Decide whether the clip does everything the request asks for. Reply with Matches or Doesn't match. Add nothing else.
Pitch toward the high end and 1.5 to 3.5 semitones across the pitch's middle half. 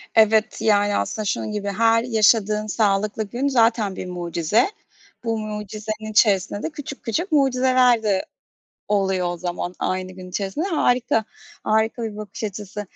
Matches